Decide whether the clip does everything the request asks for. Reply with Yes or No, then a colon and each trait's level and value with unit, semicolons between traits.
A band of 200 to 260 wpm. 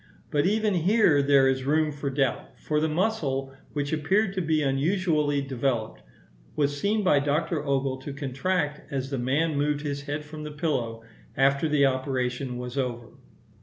No: average, 165 wpm